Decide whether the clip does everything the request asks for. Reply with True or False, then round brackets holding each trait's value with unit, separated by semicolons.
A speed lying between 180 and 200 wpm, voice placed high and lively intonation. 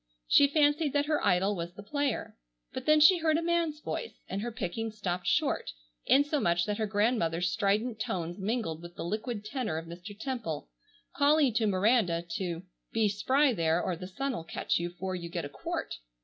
True (190 wpm; 210 Hz; 7.6 semitones)